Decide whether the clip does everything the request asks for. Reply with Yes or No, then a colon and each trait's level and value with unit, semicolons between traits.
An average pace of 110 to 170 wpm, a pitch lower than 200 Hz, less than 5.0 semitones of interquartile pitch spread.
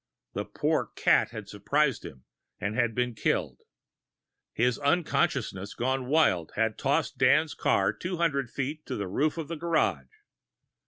No: average, 145 wpm; low, 135 Hz; wide, 5.5 semitones